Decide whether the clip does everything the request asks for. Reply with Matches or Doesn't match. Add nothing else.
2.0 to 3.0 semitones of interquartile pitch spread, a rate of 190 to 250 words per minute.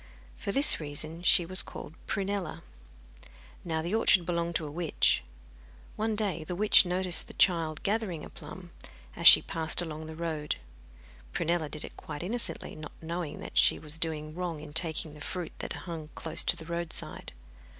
Doesn't match